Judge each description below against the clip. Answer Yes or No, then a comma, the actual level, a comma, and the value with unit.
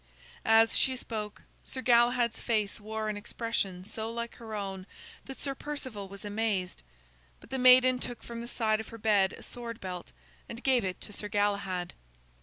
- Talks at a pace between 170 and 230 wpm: Yes, average, 180 wpm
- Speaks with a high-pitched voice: Yes, high, 220 Hz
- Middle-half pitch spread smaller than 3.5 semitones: Yes, average, 2.9 semitones